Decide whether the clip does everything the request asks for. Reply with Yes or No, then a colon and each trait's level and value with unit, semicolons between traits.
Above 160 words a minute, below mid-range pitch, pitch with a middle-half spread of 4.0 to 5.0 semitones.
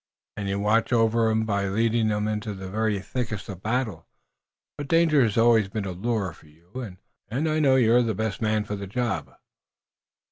No: average, 200 wpm; low, 110 Hz; average, 2.8 semitones